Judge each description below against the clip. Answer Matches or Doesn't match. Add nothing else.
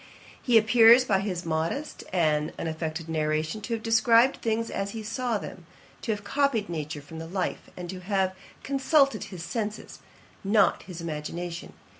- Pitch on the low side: Doesn't match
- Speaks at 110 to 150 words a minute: Doesn't match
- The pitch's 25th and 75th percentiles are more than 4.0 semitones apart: Matches